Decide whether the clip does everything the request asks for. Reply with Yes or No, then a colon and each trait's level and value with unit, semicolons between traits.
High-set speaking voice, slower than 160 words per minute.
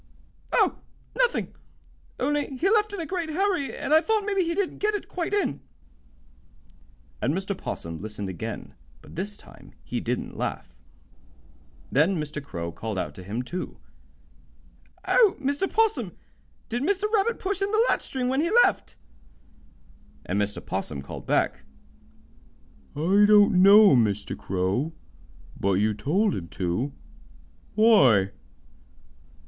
Yes: high, 205 Hz; average, 140 wpm